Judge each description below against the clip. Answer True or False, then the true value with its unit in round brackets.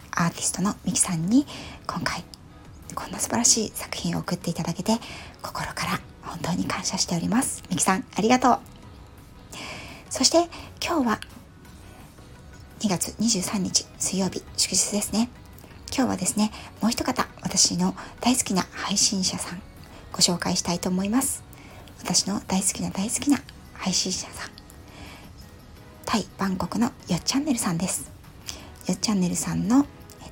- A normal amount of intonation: True (4.6 semitones)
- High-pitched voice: True (200 Hz)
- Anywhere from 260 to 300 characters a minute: True (290 characters per minute)